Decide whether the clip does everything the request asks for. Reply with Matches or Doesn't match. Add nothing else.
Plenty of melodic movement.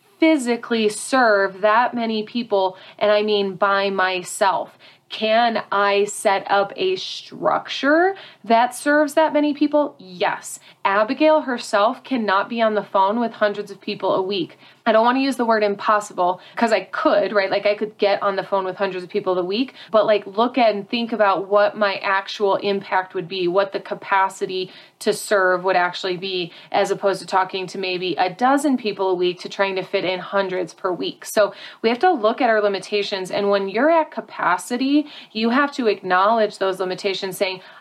Doesn't match